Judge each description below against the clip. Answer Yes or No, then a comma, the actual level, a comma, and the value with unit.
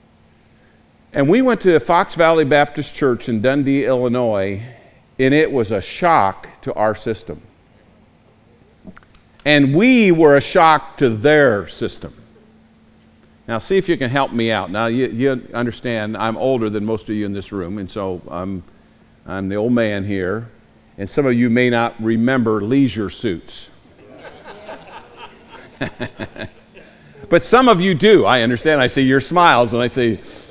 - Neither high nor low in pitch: No, low, 120 Hz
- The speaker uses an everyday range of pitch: Yes, average, 4.8 semitones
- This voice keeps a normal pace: Yes, average, 155 wpm